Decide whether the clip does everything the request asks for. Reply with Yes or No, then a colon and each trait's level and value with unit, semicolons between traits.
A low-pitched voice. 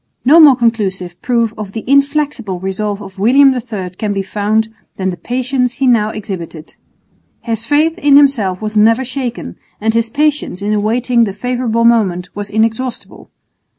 No: high, 225 Hz